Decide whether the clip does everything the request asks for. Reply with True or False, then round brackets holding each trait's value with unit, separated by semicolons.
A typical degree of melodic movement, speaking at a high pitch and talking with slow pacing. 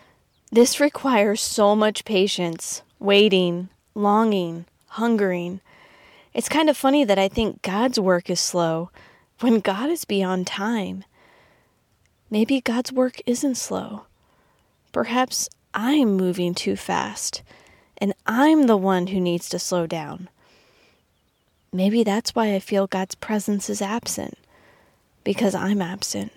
True (4.0 semitones; 205 Hz; 125 wpm)